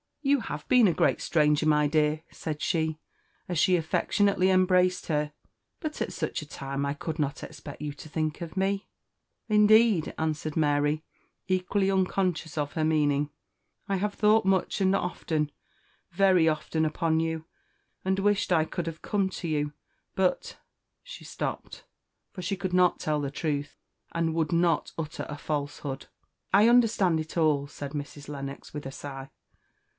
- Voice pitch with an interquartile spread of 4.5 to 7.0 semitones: No, average, 4.1 semitones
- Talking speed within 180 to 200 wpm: No, average, 165 wpm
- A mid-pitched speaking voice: Yes, medium, 160 Hz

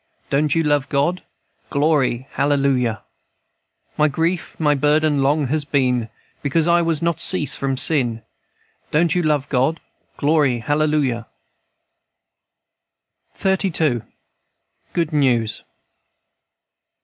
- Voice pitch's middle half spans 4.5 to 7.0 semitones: No, average, 2.9 semitones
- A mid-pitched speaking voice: Yes, medium, 145 Hz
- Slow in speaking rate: Yes, slow, 100 wpm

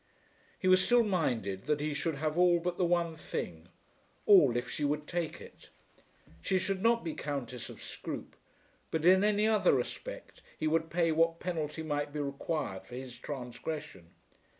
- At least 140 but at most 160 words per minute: No, average, 175 wpm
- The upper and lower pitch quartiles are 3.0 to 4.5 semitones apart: Yes, average, 4.1 semitones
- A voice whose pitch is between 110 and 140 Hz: No, medium, 160 Hz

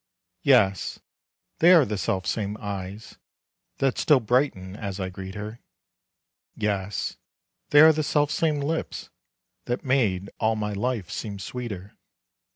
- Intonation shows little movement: No, wide, 5.5 semitones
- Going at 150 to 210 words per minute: No, slow, 135 wpm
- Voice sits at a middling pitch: No, low, 105 Hz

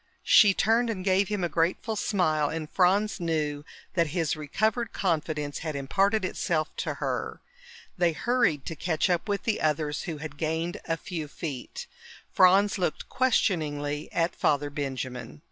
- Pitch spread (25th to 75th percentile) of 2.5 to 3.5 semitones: No, average, 4.5 semitones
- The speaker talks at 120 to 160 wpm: Yes, average, 155 wpm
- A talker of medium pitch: Yes, medium, 165 Hz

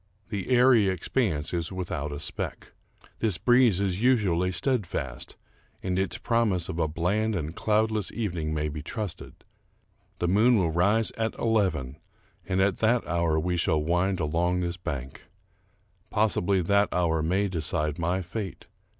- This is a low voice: Yes, very low, 90 Hz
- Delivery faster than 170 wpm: No, average, 150 wpm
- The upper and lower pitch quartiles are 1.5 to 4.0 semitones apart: No, average, 4.5 semitones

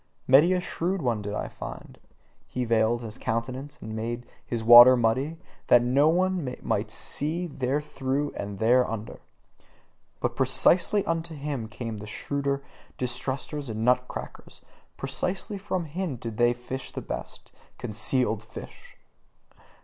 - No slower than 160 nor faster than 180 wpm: No, slow, 135 wpm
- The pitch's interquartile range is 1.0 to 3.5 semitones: No, average, 4.4 semitones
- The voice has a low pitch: Yes, low, 125 Hz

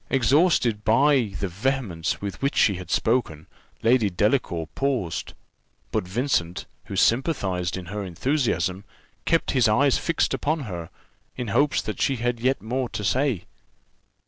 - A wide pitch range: Yes, wide, 6.3 semitones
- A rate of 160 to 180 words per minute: No, average, 145 wpm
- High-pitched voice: No, low, 115 Hz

